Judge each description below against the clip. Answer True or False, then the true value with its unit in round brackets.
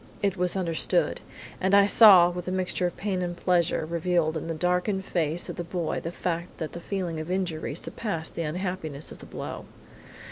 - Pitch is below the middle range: False (175 Hz)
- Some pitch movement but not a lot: False (2.1 semitones)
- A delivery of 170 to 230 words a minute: True (200 wpm)